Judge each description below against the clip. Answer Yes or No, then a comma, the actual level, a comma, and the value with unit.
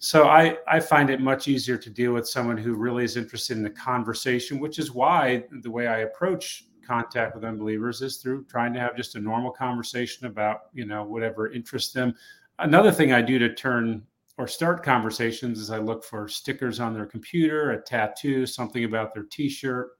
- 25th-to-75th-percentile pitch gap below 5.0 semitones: Yes, average, 2.7 semitones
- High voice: No, low, 120 Hz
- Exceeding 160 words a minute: Yes, average, 200 wpm